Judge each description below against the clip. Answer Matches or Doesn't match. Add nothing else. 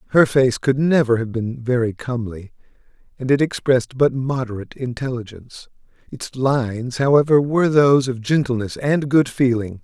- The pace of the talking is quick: Doesn't match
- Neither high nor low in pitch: Doesn't match